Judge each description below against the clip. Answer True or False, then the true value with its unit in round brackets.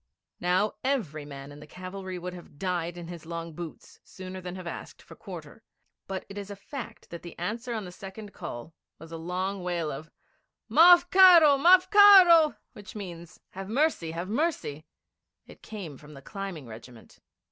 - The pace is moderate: True (180 wpm)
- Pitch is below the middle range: False (185 Hz)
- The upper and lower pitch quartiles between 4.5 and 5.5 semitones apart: True (4.9 semitones)